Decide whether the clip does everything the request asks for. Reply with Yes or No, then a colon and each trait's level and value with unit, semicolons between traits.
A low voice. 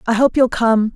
No: high, 235 Hz